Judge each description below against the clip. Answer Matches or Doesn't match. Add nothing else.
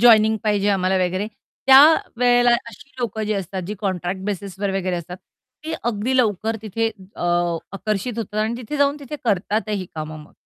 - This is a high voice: Matches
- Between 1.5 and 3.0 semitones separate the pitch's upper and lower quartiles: Doesn't match